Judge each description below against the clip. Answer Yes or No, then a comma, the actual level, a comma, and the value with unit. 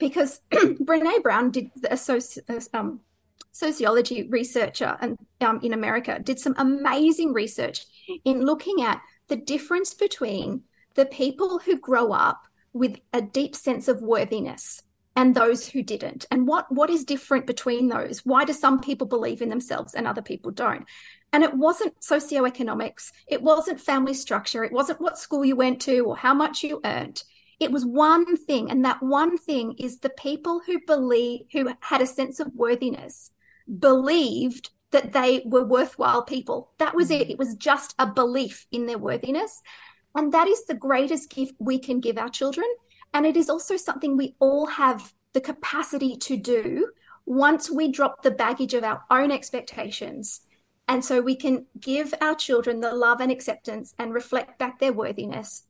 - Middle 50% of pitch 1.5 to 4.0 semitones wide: Yes, average, 3.4 semitones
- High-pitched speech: Yes, very high, 270 Hz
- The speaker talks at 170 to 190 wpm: Yes, average, 175 wpm